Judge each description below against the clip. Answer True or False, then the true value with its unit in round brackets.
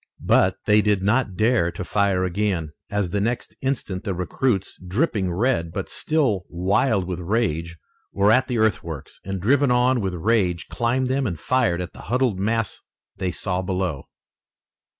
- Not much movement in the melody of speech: False (4.8 semitones)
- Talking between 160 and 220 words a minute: True (165 wpm)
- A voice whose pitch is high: False (100 Hz)